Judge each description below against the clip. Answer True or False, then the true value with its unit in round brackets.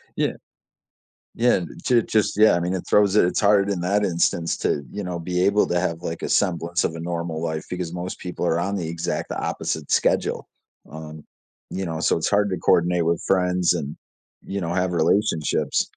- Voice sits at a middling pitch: False (90 Hz)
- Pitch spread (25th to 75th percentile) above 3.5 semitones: False (2.7 semitones)